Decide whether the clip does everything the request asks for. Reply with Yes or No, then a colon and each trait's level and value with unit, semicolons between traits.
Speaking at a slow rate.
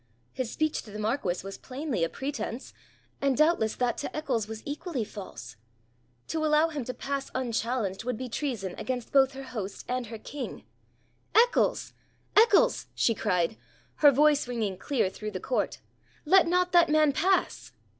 No: average, 165 wpm